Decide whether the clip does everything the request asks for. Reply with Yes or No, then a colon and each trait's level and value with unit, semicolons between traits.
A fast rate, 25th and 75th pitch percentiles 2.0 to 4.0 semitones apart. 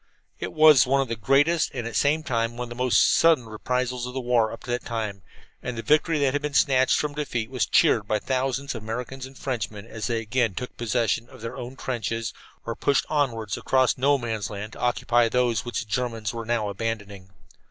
Yes: fast, 225 wpm; average, 2.7 semitones